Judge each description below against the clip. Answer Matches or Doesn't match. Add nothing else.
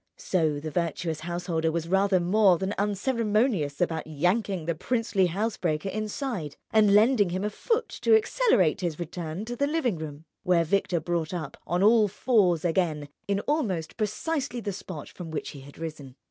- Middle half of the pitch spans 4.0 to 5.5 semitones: Matches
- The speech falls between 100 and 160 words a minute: Doesn't match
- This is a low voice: Doesn't match